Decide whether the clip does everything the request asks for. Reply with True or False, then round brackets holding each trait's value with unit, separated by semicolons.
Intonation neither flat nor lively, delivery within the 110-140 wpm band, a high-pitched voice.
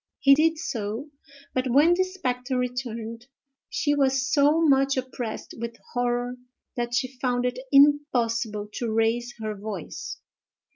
True (3.0 semitones; 135 wpm; 250 Hz)